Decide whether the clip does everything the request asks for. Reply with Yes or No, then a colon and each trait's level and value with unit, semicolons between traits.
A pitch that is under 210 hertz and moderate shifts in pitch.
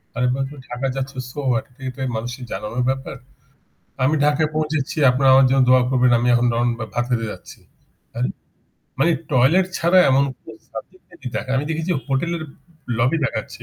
Yes: low, 135 Hz; average, 3.1 semitones